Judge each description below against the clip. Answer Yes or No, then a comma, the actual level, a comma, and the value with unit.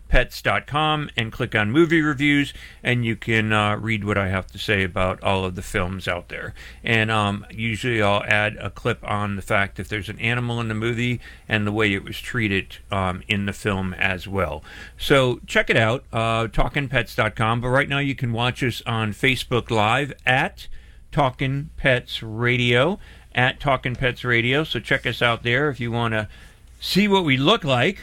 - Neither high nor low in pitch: No, low, 115 Hz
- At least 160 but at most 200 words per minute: Yes, average, 195 wpm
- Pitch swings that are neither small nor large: Yes, average, 3.6 semitones